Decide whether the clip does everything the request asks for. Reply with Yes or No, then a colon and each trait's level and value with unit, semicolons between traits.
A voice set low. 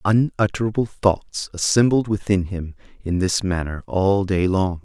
Yes: very low, 95 Hz